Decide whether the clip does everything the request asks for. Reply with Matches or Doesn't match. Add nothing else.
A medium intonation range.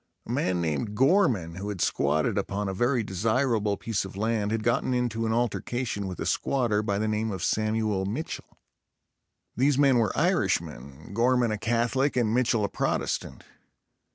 Matches